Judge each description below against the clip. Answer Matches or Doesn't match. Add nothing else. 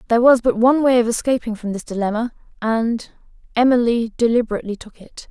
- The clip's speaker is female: Matches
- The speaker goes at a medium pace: Matches